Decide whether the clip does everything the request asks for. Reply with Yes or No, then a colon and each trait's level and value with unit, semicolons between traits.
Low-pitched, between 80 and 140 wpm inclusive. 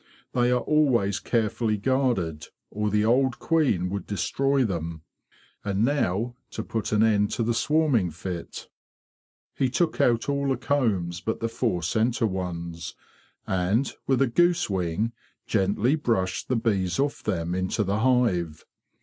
No: low, 110 Hz; average, 150 wpm